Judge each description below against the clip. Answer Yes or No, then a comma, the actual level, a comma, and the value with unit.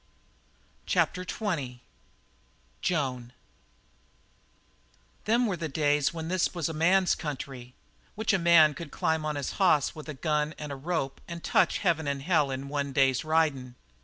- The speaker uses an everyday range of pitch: Yes, average, 3.6 semitones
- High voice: No, medium, 155 Hz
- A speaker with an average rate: Yes, average, 155 wpm